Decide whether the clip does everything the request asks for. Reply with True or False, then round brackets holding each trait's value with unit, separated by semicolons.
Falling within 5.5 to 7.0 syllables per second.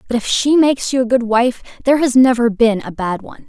True (6.2 syllables/s)